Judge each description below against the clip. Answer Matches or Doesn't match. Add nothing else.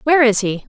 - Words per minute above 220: Matches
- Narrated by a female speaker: Matches